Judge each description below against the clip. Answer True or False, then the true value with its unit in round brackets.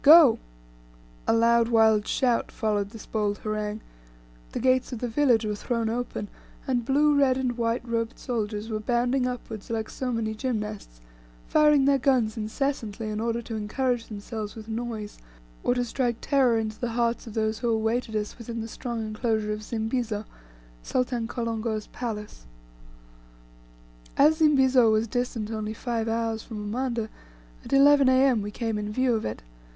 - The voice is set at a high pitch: True (230 Hz)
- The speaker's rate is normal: True (165 wpm)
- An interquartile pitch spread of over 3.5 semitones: False (2.5 semitones)